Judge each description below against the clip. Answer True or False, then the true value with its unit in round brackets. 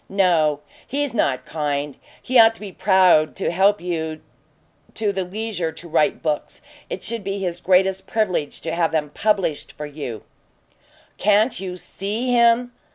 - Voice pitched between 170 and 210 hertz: True (185 Hz)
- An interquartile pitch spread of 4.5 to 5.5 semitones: True (5.0 semitones)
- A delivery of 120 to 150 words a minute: False (160 wpm)